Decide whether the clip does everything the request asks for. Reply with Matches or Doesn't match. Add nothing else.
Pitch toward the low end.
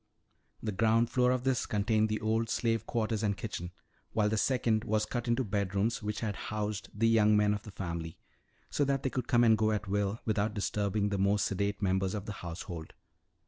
Matches